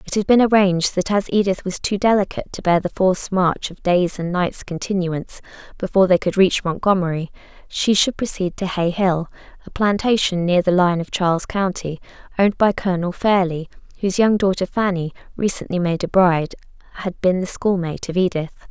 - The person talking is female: Yes, female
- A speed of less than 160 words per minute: No, average, 185 wpm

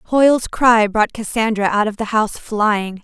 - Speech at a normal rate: Yes, average, 180 wpm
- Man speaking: No, female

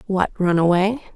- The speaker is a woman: Yes, female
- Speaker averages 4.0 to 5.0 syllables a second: Yes, 4.4 syllables/s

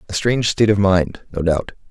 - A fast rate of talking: Yes, fast, 220 wpm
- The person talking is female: No, male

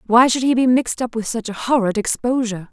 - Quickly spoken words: Yes, fast, 245 wpm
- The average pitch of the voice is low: No, high, 235 Hz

